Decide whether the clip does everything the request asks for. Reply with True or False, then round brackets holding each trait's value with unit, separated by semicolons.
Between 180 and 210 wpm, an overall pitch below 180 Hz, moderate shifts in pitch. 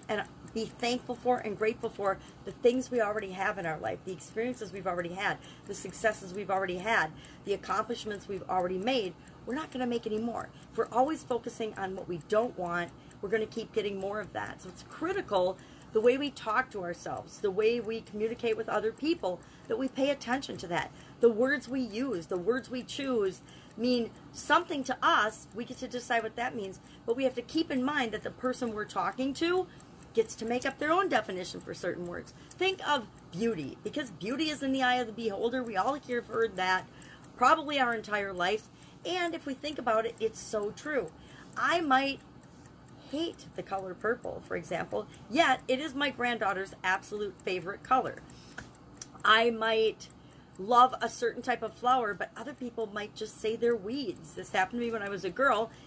False (200 wpm; 230 Hz; 4.1 semitones)